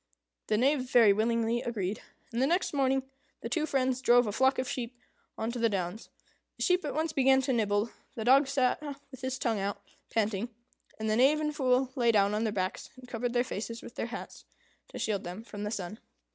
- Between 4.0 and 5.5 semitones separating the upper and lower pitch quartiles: No, average, 3.4 semitones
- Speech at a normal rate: No, fast, 215 wpm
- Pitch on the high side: Yes, high, 240 Hz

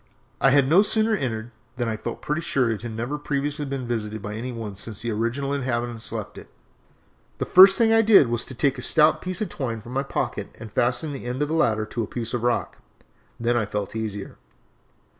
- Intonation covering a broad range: No, average, 4.3 semitones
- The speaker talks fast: Yes, fast, 225 wpm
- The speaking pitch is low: Yes, low, 120 Hz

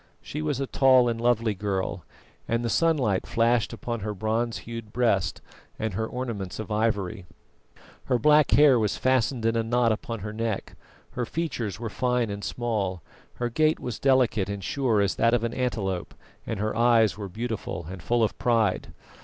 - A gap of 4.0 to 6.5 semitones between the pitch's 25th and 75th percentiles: No, average, 2.9 semitones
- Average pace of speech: Yes, average, 180 wpm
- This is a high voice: No, low, 115 Hz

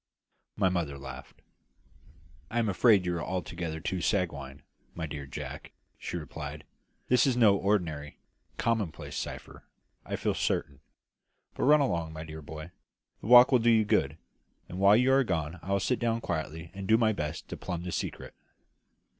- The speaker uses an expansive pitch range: Yes, wide, 5.9 semitones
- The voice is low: Yes, very low, 90 Hz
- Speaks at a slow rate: No, average, 170 wpm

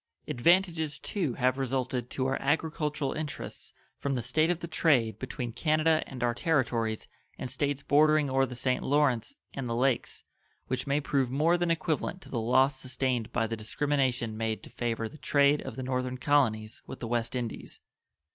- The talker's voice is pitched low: Yes, low, 130 Hz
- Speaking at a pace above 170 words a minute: Yes, average, 180 wpm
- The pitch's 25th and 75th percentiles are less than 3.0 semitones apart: No, average, 3.7 semitones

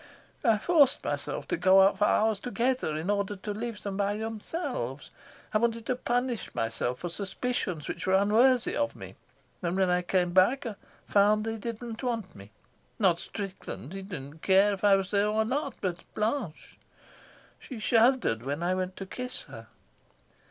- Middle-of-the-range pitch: No, high, 205 Hz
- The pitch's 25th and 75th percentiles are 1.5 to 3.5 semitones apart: No, average, 4.1 semitones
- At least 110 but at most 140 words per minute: No, average, 175 wpm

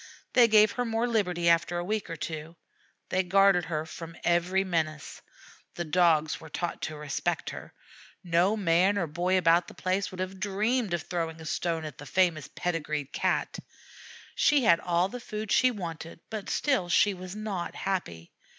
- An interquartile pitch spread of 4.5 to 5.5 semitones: No, average, 3.2 semitones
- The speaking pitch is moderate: Yes, medium, 175 Hz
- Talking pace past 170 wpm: Yes, average, 180 wpm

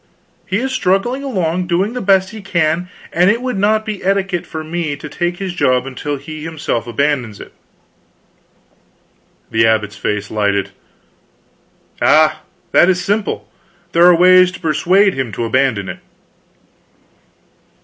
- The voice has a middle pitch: Yes, medium, 175 Hz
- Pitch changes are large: Yes, wide, 5.8 semitones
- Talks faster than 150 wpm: No, average, 145 wpm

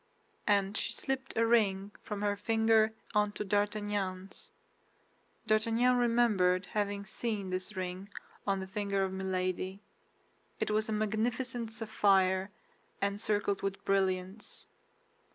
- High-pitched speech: Yes, high, 205 Hz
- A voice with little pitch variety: Yes, narrow, 2.3 semitones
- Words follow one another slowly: Yes, slow, 115 wpm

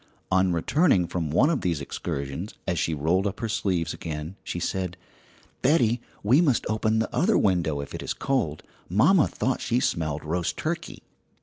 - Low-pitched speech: Yes, very low, 95 Hz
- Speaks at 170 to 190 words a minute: Yes, average, 175 wpm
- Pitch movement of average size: No, wide, 6.3 semitones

